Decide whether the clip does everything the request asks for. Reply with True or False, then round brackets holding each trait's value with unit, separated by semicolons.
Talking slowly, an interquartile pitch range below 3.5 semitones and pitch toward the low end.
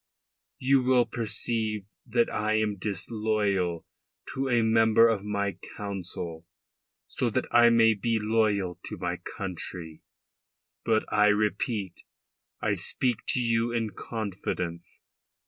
True (120 wpm; 2.7 semitones; 110 Hz)